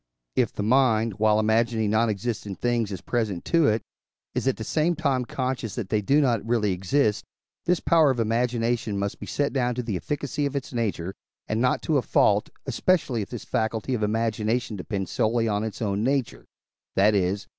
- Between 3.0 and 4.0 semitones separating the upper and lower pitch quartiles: Yes, average, 3.3 semitones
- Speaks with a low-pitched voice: Yes, low, 115 Hz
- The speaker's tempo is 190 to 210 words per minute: Yes, average, 200 wpm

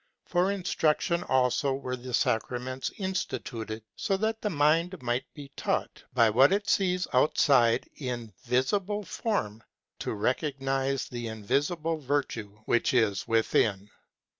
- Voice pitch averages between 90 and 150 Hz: Yes, low, 135 Hz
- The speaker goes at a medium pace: No, slow, 130 wpm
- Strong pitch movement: Yes, wide, 6.3 semitones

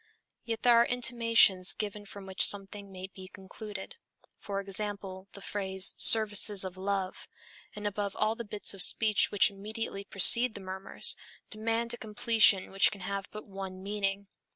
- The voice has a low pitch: No, high, 200 Hz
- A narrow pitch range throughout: Yes, narrow, 2.0 semitones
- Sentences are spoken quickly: No, average, 160 wpm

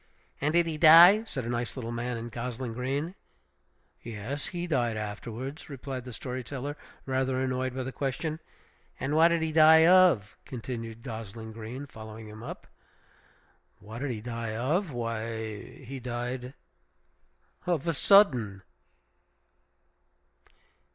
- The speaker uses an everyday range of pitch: Yes, average, 4.3 semitones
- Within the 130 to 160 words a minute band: Yes, slow, 135 wpm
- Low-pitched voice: Yes, low, 125 Hz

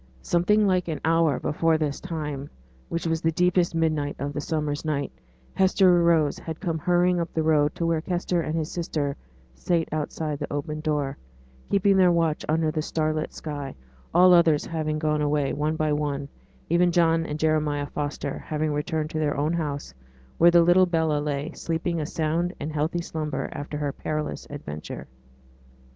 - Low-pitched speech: No, medium, 155 Hz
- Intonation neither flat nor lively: No, narrow, 2.2 semitones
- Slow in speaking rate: No, average, 180 wpm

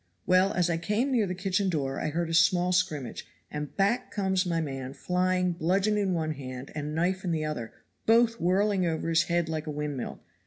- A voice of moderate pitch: Yes, medium, 175 Hz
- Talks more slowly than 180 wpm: No, fast, 205 wpm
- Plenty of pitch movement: No, average, 3.6 semitones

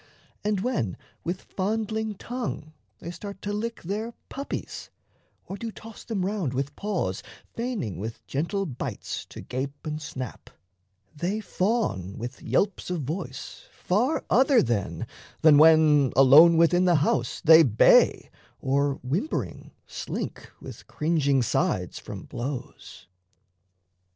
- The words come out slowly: Yes, slow, 125 wpm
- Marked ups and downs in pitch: Yes, wide, 7.3 semitones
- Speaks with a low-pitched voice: No, medium, 165 Hz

